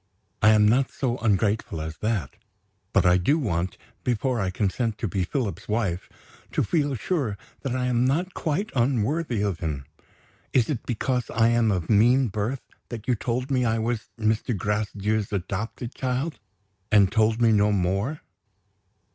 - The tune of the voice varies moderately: Yes, average, 3.8 semitones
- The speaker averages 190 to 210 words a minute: No, average, 165 wpm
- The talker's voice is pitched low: Yes, low, 110 Hz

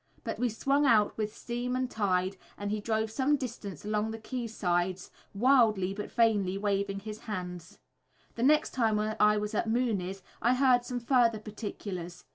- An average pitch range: Yes, average, 3.4 semitones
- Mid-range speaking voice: No, high, 215 Hz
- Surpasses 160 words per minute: Yes, average, 170 wpm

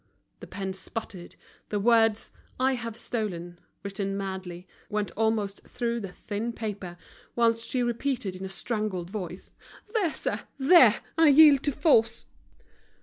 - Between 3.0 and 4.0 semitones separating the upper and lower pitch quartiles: Yes, average, 3.7 semitones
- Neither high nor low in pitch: No, high, 215 Hz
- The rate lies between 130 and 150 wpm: Yes, average, 140 wpm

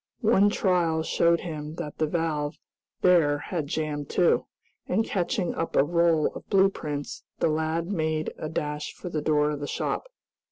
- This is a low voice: No, medium, 160 Hz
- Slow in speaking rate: No, average, 170 wpm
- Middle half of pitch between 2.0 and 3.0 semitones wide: Yes, average, 2.7 semitones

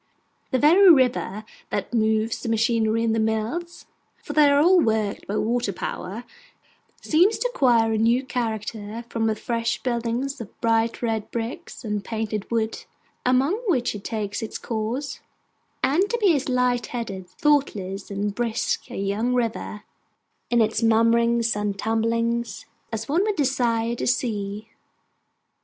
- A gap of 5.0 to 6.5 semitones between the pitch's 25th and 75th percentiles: No, narrow, 2.5 semitones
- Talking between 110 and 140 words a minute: No, average, 150 wpm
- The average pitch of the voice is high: Yes, high, 230 Hz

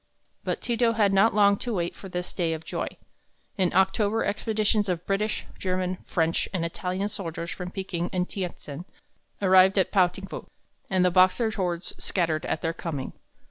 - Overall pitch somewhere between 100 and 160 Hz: No, medium, 185 Hz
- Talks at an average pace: Yes, average, 180 wpm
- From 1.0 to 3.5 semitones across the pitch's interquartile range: Yes, narrow, 2.4 semitones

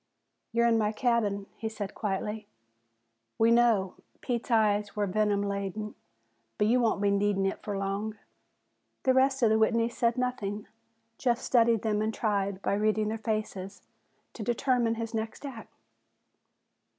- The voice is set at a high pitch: Yes, high, 215 Hz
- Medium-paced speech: Yes, average, 150 wpm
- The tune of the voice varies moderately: No, narrow, 2.2 semitones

